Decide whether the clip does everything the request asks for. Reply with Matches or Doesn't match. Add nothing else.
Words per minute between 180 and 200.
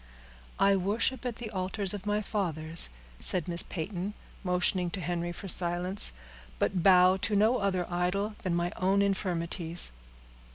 Doesn't match